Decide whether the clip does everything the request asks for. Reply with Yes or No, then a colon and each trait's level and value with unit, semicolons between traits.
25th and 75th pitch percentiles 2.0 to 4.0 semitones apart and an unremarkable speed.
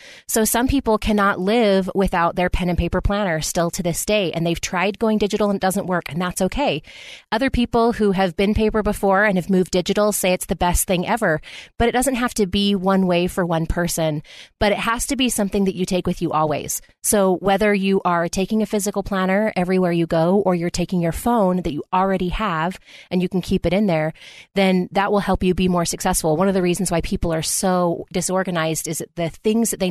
No: average, 2.9 semitones; fast, 235 wpm